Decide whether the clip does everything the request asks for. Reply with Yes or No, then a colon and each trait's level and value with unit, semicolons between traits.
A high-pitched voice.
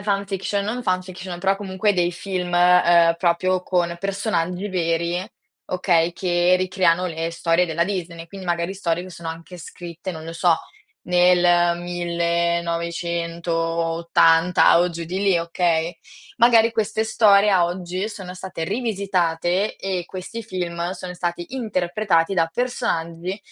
No: medium, 175 Hz